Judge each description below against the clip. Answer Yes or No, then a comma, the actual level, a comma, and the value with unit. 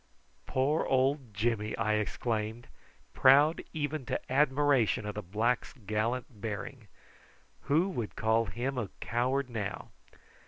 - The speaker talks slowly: Yes, slow, 120 wpm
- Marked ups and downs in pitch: No, average, 4.1 semitones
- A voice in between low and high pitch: No, low, 120 Hz